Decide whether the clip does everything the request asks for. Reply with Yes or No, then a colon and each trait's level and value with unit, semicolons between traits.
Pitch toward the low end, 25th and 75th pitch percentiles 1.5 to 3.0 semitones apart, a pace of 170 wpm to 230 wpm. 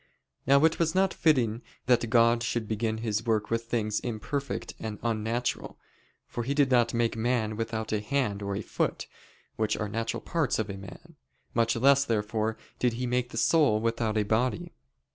Yes: low, 115 Hz; narrow, 2.4 semitones; average, 180 wpm